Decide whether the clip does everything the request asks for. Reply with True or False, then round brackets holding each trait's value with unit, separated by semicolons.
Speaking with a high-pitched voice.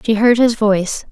True (220 Hz)